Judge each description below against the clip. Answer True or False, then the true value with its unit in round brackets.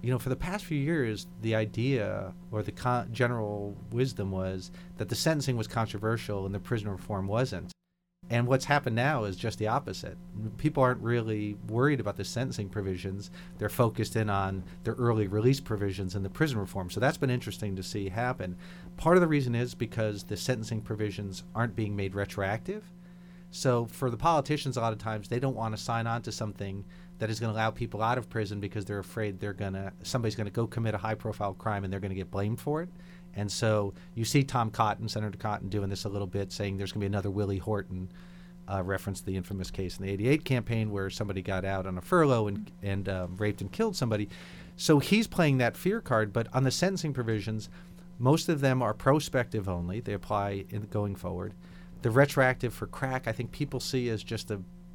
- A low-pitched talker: True (110 Hz)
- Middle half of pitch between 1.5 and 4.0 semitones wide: False (4.4 semitones)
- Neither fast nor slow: False (215 wpm)